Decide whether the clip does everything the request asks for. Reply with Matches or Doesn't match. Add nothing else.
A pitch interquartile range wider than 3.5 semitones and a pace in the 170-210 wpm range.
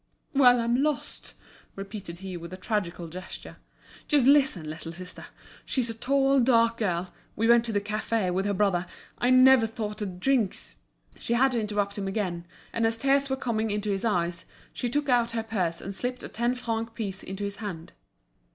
Matches